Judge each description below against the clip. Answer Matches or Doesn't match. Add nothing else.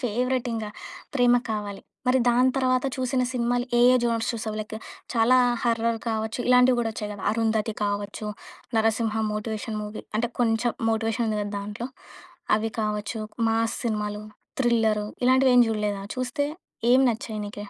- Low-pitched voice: Doesn't match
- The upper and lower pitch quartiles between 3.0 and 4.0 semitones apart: Doesn't match